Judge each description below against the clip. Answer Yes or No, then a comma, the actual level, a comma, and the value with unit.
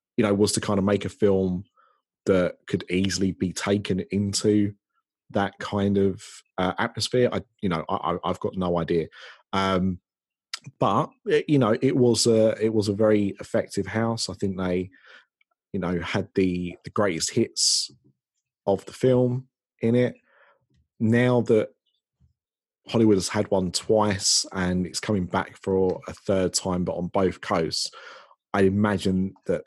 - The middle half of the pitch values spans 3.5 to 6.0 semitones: No, average, 2.8 semitones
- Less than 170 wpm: Yes, average, 160 wpm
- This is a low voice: Yes, low, 100 Hz